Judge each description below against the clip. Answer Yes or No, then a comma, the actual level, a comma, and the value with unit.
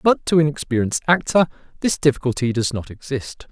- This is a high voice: No, medium, 140 Hz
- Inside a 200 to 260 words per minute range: No, average, 170 wpm